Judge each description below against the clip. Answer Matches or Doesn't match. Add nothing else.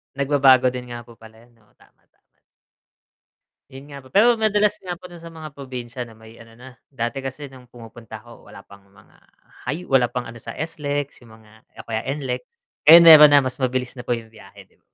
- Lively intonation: Doesn't match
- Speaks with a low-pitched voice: Matches